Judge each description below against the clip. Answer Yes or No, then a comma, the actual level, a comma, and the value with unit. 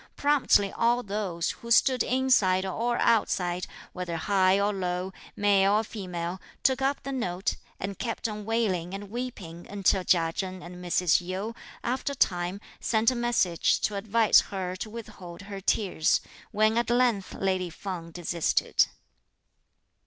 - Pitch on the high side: Yes, high, 195 Hz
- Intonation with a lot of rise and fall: No, average, 4.1 semitones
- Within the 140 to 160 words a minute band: Yes, average, 150 wpm